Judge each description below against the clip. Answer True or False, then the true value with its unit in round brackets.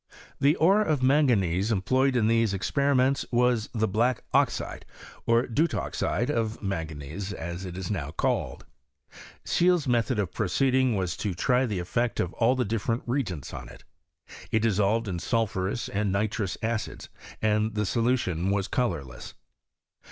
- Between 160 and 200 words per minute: False (150 wpm)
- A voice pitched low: True (110 Hz)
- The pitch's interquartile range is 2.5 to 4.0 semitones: False (4.5 semitones)